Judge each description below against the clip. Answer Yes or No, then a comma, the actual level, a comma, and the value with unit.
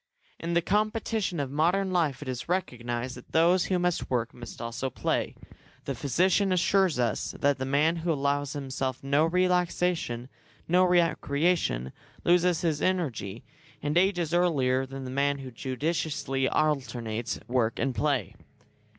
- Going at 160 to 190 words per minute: No, average, 145 wpm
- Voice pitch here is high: No, medium, 145 Hz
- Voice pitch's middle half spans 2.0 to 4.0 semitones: No, average, 5.3 semitones